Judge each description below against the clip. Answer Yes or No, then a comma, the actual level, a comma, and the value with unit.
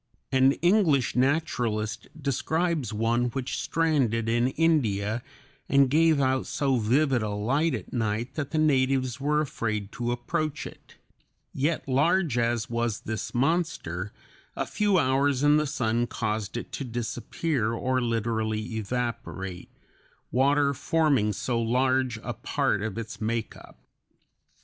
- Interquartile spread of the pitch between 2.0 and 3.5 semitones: No, average, 4.2 semitones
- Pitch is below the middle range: Yes, low, 125 Hz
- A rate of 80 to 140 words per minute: Yes, slow, 135 wpm